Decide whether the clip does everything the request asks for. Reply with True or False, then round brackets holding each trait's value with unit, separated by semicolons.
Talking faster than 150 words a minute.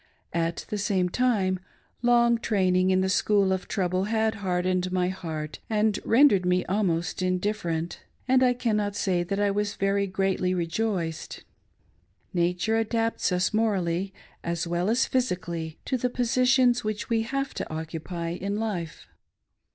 False (145 wpm)